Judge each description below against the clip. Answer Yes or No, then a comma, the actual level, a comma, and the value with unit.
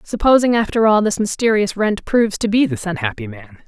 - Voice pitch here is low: No, high, 220 Hz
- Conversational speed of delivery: Yes, average, 195 wpm